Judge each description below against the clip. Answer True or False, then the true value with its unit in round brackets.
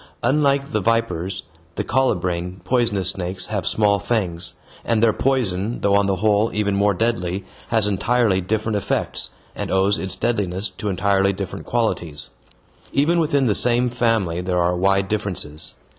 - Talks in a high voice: False (100 Hz)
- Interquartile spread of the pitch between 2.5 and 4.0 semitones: True (3.7 semitones)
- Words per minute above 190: False (155 wpm)